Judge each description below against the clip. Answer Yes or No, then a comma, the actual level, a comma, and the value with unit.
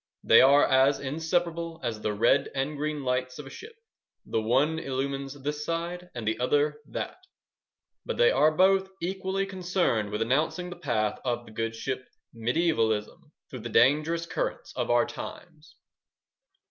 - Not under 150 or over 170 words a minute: Yes, average, 160 wpm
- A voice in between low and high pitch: Yes, medium, 145 Hz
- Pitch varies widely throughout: Yes, wide, 5.7 semitones